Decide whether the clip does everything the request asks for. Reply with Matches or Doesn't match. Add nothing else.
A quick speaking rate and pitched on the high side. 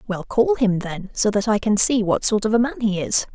Matches